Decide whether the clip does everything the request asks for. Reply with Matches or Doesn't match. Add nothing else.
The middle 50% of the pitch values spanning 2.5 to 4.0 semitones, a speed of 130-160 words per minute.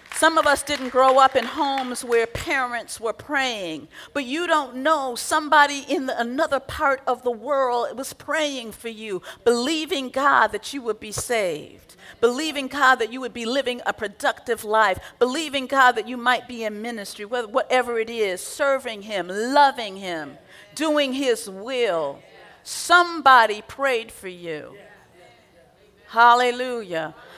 Matches